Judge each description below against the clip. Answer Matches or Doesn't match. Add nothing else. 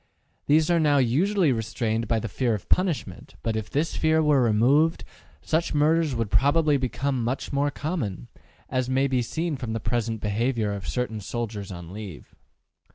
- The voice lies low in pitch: Matches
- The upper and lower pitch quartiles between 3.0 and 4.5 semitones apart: Doesn't match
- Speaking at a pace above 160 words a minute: Matches